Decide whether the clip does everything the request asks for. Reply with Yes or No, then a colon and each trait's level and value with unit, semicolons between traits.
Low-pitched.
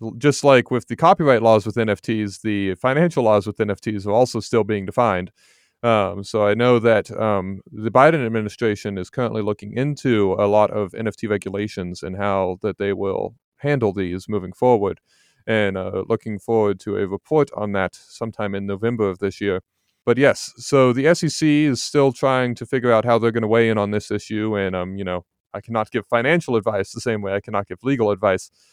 Yes: low, 110 Hz